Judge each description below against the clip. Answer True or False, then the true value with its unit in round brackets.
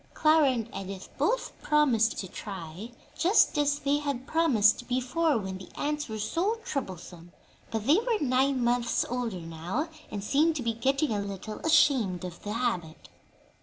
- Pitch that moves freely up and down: True (6.7 semitones)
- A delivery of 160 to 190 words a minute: True (165 wpm)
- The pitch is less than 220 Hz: False (245 Hz)